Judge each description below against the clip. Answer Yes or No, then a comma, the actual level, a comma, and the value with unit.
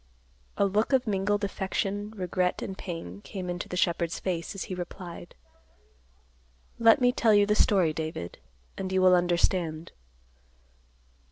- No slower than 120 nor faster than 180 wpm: Yes, average, 145 wpm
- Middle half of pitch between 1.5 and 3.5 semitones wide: Yes, average, 2.8 semitones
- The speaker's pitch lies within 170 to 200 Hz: Yes, medium, 185 Hz